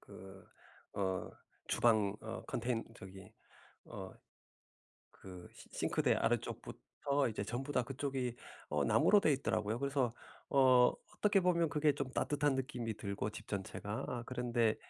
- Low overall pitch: Yes, low, 120 Hz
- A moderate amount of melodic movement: Yes, average, 4.9 semitones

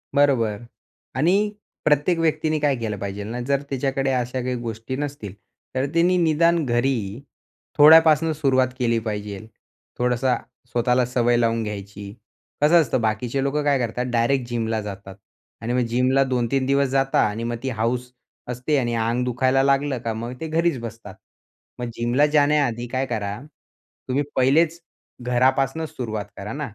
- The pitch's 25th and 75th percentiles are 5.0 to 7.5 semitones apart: No, average, 3.3 semitones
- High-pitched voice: No, low, 125 Hz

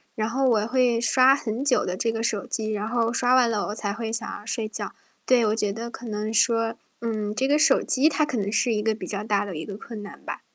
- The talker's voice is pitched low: No, high, 225 Hz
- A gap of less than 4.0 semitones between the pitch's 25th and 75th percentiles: Yes, narrow, 2.5 semitones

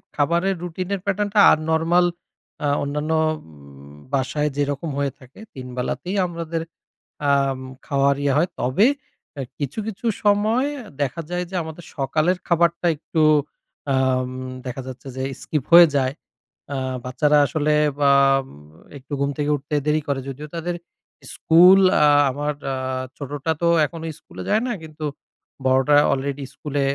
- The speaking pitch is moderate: Yes, medium, 150 Hz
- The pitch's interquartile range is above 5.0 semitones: No, average, 3.9 semitones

